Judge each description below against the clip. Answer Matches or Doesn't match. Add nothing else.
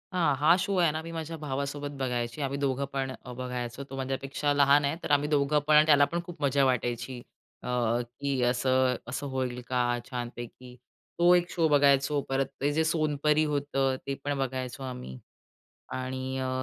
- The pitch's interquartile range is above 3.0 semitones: Doesn't match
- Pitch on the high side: Doesn't match